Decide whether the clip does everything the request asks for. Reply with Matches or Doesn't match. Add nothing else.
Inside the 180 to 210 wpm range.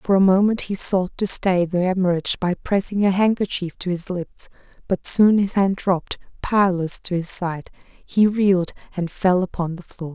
Matches